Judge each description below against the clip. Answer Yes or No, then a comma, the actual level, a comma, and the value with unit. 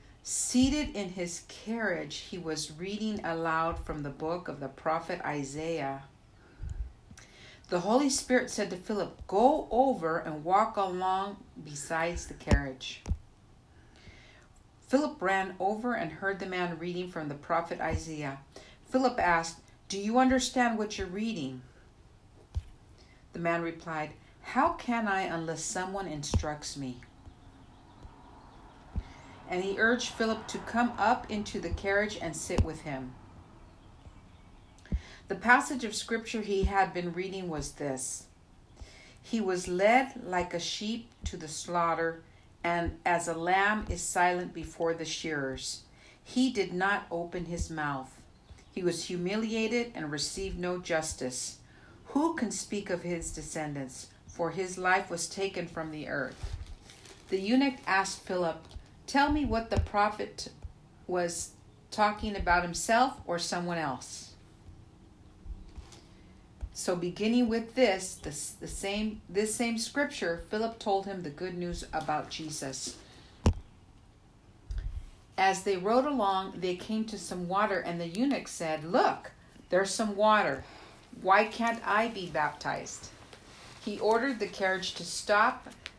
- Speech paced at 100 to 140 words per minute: Yes, slow, 135 wpm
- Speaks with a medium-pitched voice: Yes, medium, 175 Hz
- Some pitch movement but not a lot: No, wide, 7.1 semitones